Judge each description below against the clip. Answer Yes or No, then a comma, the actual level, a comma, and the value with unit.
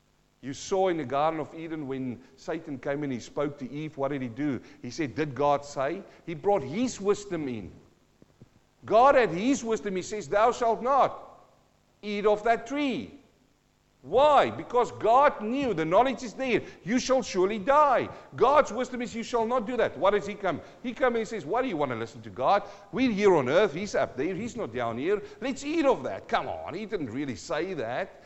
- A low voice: No, high, 205 Hz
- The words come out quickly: Yes, fast, 215 wpm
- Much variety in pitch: Yes, wide, 8.9 semitones